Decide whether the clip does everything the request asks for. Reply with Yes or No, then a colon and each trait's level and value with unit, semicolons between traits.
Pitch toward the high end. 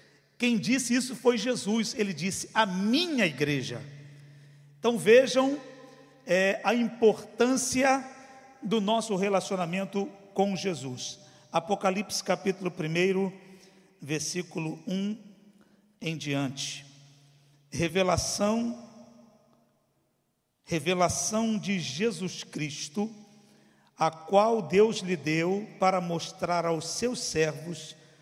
Yes: high, 195 Hz